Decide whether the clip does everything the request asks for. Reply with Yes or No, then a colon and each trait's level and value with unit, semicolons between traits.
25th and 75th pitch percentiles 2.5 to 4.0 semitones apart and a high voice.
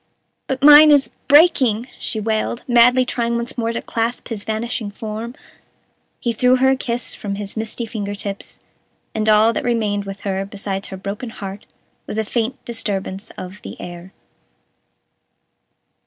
Yes: average, 3.0 semitones; high, 220 Hz